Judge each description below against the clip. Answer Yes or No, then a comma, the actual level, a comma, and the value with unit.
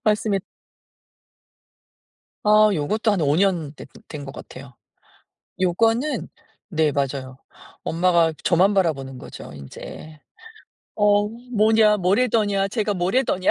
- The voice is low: No, high, 190 Hz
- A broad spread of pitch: Yes, wide, 5.7 semitones